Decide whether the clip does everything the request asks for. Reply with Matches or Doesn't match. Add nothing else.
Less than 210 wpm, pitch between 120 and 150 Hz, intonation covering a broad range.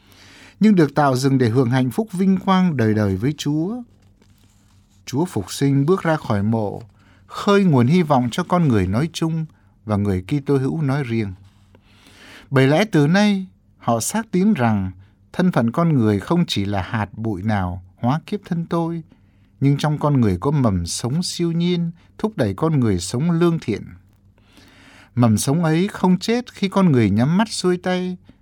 Matches